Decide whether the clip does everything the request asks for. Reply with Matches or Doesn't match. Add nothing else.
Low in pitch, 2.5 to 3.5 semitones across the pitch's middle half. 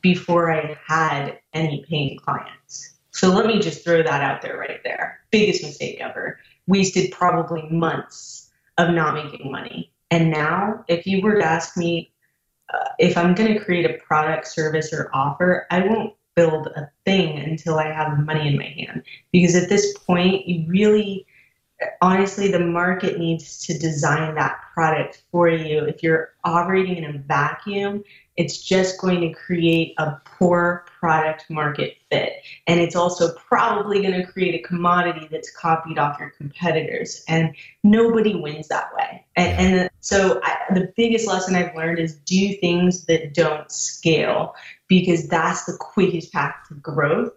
Doesn't match